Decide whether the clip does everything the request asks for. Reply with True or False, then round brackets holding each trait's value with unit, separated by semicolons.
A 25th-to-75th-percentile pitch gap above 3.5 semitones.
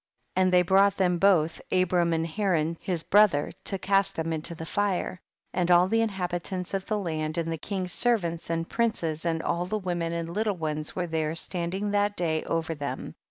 False (3.0 semitones)